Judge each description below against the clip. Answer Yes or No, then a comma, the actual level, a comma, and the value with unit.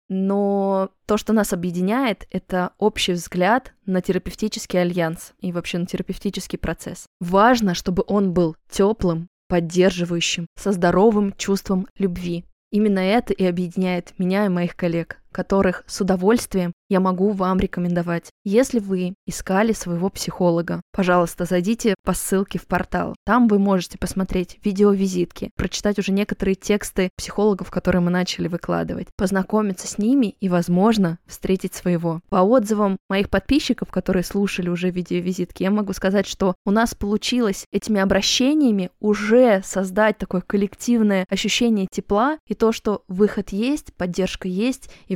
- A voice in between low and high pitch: No, high, 195 Hz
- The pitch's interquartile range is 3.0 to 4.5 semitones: No, narrow, 2.4 semitones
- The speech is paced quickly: No, average, 140 wpm